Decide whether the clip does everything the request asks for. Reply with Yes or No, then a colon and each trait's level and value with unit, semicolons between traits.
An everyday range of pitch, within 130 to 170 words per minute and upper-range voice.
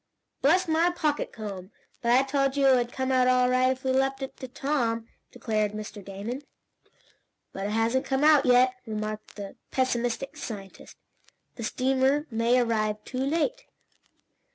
Yes: average, 3.3 semitones; average, 160 wpm; very high, 255 Hz